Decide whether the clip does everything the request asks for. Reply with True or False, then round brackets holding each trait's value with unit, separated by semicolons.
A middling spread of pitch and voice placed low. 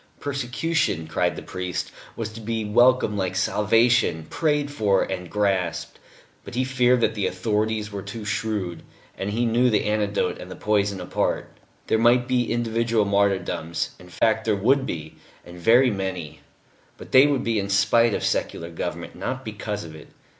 True (3.9 semitones; 105 Hz)